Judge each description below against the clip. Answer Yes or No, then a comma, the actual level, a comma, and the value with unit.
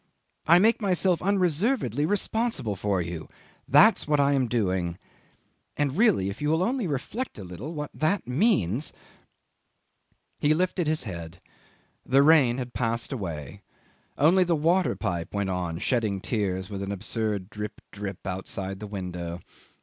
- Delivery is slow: No, average, 150 wpm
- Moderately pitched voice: No, low, 125 Hz